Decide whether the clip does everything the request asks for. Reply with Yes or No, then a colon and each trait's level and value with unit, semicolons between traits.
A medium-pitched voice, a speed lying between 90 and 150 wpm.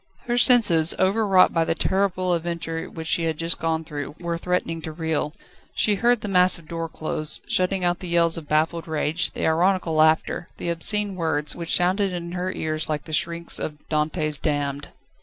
No: medium, 170 Hz; average, 185 wpm